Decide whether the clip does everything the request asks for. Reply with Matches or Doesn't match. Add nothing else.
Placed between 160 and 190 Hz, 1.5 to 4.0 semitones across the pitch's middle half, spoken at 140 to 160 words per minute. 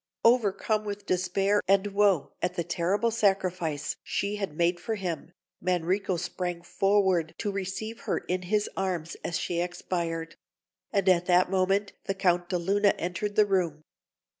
Matches